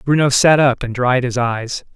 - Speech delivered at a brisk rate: Yes, fast, 215 wpm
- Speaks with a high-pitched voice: No, low, 130 Hz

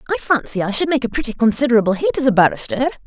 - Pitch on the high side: Yes, high, 245 Hz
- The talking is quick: Yes, fast, 235 wpm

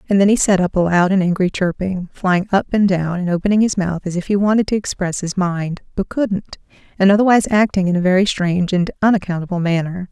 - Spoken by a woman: Yes, female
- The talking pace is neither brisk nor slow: No, fast, 225 wpm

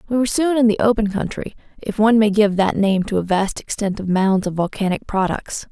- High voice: Yes, high, 205 Hz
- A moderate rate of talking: No, fast, 230 wpm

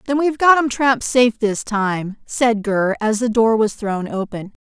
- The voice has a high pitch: Yes, high, 225 Hz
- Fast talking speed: Yes, fast, 210 wpm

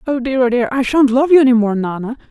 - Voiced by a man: No, female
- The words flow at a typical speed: No, fast, 285 wpm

